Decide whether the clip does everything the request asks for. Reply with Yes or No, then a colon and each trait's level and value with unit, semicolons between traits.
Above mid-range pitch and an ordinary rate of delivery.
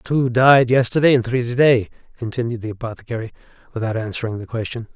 No: low, 120 Hz; average, 170 wpm